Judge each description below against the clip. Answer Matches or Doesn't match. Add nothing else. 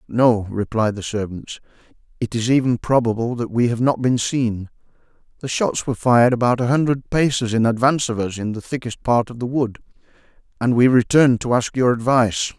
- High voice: Doesn't match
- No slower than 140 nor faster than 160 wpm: Doesn't match